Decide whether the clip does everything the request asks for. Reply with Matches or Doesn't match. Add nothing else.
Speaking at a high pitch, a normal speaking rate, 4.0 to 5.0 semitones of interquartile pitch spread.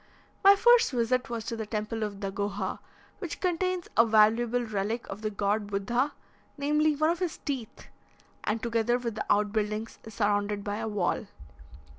Doesn't match